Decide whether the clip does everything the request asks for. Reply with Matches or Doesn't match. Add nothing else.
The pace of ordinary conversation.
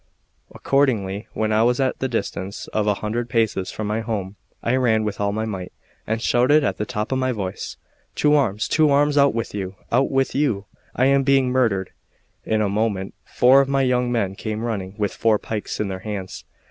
Doesn't match